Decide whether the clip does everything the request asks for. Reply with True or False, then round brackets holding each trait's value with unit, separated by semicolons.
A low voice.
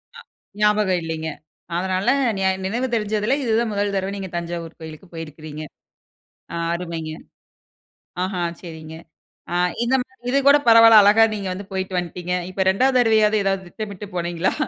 False (190 Hz)